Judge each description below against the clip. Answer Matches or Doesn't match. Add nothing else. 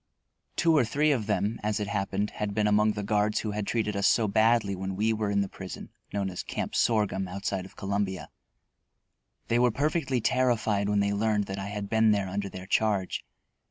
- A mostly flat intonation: Matches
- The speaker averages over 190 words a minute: Matches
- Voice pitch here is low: Matches